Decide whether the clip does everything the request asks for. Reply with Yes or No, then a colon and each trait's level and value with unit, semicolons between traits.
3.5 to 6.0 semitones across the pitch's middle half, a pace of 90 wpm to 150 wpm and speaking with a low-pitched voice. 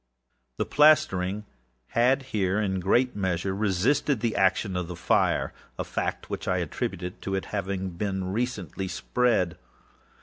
Yes: average, 4.0 semitones; slow, 135 wpm; very low, 95 Hz